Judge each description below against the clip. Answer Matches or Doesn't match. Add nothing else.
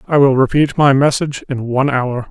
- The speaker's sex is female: Doesn't match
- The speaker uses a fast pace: Matches